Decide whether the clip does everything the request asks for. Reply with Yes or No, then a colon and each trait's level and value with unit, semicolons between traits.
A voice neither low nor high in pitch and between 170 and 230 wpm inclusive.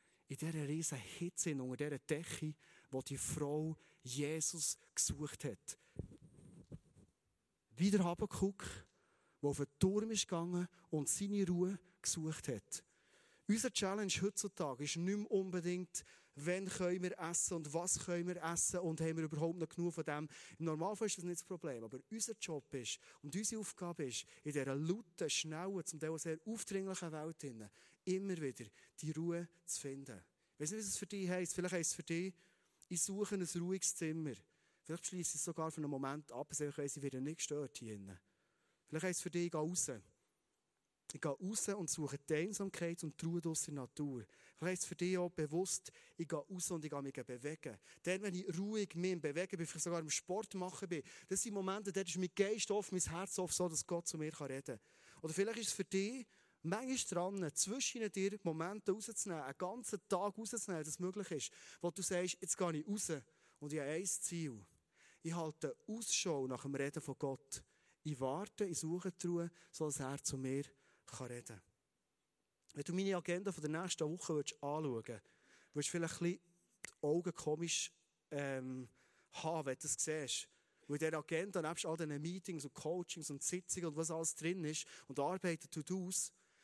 Yes: medium, 170 Hz; fast, 190 wpm